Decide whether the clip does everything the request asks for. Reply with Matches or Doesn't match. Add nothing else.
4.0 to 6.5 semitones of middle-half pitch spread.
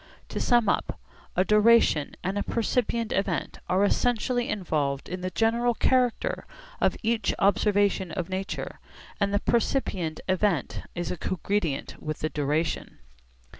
Matches